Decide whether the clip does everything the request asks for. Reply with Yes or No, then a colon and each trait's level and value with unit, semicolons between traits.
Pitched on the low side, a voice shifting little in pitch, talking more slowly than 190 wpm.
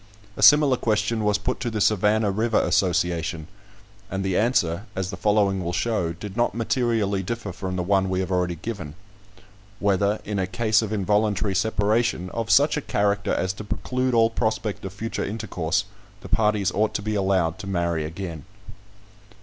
No: low, 100 Hz; average, 3.0 semitones; average, 175 wpm